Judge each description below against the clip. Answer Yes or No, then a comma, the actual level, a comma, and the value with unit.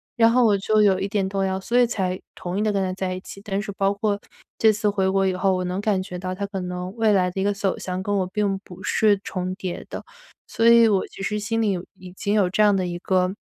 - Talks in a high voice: Yes, high, 195 Hz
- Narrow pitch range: Yes, narrow, 2.0 semitones